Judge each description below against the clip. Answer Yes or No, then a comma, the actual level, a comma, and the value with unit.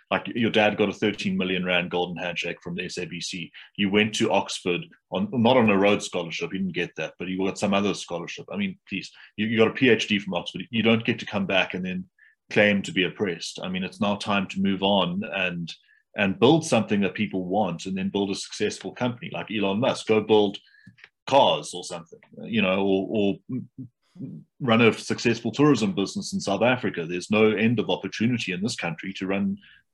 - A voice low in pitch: Yes, low, 100 Hz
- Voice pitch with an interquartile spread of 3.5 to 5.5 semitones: No, average, 2.8 semitones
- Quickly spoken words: Yes, fast, 210 wpm